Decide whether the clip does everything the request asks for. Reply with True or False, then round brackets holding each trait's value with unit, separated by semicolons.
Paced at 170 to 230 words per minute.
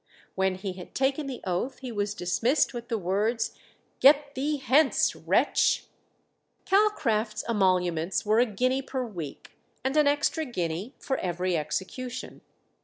False (140 wpm)